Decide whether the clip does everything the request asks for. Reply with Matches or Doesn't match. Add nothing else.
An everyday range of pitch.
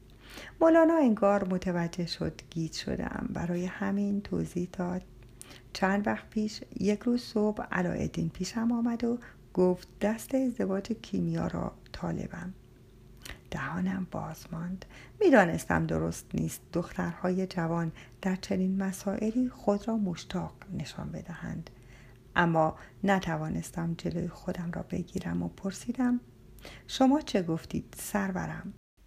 Matches